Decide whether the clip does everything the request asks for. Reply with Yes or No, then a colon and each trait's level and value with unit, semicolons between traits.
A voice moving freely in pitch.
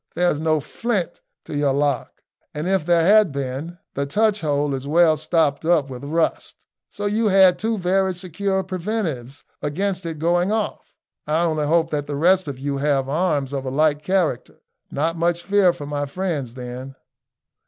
No: average, 4.5 semitones